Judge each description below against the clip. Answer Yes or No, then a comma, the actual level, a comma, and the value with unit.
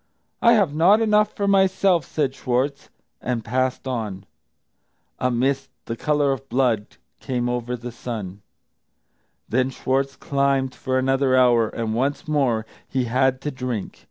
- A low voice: Yes, low, 130 Hz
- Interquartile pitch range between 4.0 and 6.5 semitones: No, narrow, 2.6 semitones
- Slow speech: No, average, 150 wpm